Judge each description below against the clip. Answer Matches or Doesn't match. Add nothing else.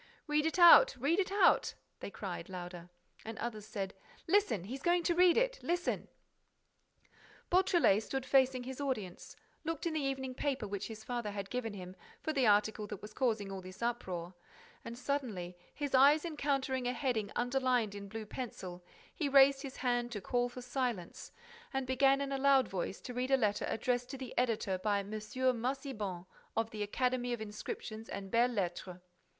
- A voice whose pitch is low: Doesn't match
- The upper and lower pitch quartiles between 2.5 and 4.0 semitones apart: Doesn't match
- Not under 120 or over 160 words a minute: Doesn't match